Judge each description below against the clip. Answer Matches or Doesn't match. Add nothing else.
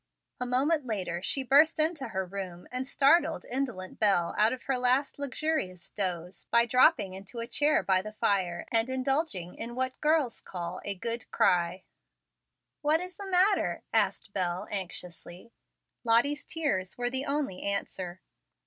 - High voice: Matches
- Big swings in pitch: Matches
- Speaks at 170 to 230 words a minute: Doesn't match